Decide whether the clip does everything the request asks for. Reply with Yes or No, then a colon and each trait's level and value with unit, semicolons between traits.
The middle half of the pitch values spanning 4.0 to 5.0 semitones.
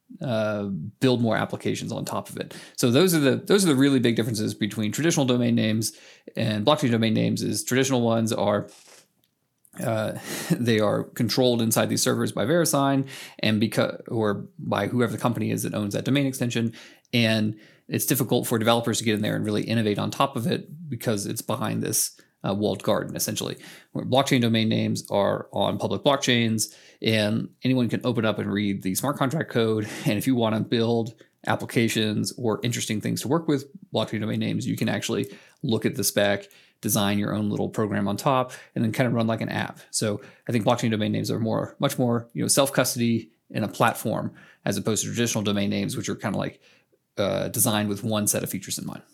No: average, 3.2 semitones